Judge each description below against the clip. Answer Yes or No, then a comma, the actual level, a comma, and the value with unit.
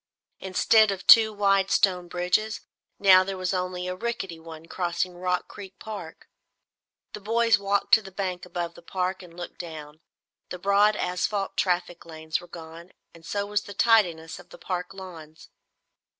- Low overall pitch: No, medium, 185 Hz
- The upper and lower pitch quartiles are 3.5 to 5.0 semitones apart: No, narrow, 2.5 semitones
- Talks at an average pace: Yes, average, 165 wpm